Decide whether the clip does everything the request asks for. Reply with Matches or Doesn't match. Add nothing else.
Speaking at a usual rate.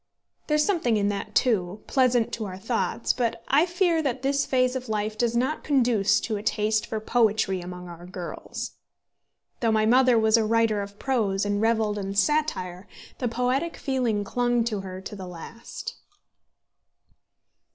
Matches